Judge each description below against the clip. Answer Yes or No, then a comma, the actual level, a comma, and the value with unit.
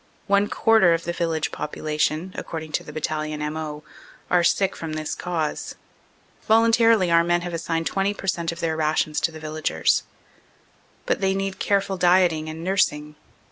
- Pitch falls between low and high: Yes, medium, 170 Hz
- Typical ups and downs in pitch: Yes, average, 3.5 semitones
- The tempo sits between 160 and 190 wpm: Yes, average, 170 wpm